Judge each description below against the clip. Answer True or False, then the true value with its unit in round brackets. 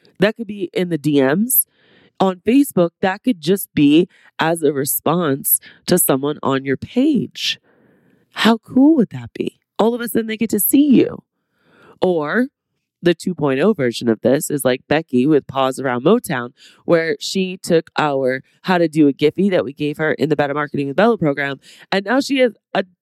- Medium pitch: True (170 Hz)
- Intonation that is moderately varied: False (6.8 semitones)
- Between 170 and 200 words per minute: True (190 wpm)